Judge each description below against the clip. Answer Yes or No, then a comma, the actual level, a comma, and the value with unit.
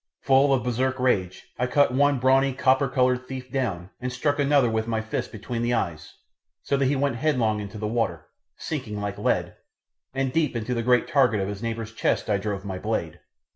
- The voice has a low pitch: Yes, low, 125 Hz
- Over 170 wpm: Yes, fast, 205 wpm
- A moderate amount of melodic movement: Yes, average, 3.6 semitones